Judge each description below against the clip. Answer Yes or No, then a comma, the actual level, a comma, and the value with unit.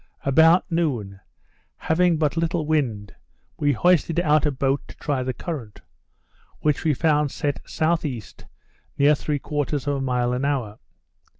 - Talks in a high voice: No, medium, 145 Hz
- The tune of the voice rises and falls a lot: No, average, 3.5 semitones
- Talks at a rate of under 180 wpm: Yes, average, 140 wpm